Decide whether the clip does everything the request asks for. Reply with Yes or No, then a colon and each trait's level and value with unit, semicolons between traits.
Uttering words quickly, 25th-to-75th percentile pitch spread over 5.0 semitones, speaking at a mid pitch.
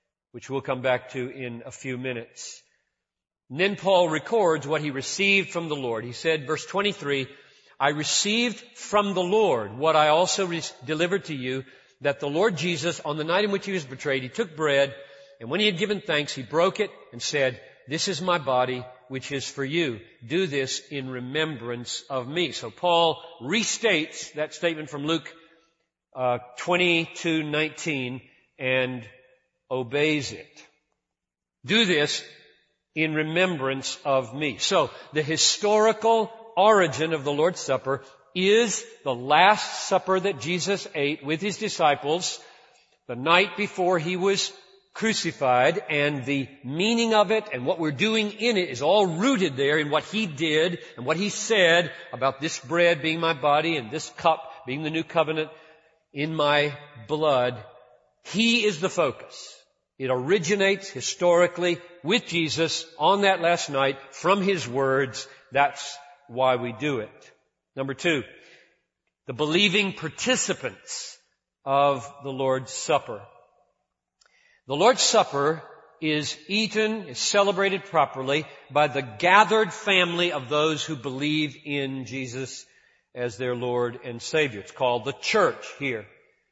No: average, 150 wpm; wide, 5.4 semitones; medium, 155 Hz